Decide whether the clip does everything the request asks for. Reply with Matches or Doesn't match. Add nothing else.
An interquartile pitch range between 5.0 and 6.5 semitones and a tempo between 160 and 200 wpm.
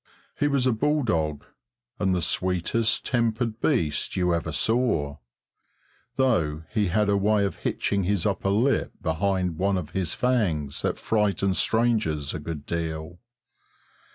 Doesn't match